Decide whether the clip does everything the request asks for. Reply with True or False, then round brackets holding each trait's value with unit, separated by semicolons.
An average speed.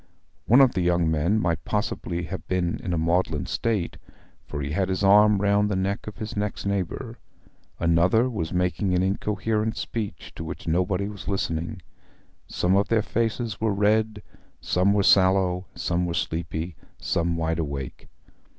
True (165 wpm)